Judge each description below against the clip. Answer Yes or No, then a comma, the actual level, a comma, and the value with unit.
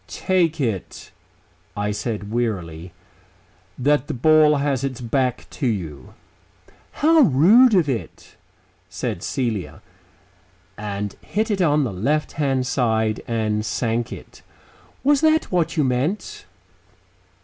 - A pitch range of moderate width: No, wide, 6.2 semitones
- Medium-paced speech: No, slow, 120 wpm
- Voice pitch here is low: Yes, low, 130 Hz